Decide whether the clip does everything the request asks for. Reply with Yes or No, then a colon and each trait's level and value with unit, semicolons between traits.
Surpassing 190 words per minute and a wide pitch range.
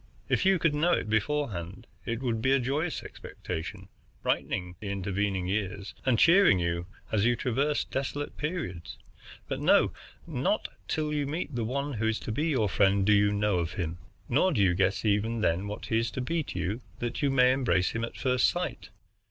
Yes: average, 200 wpm; wide, 5.9 semitones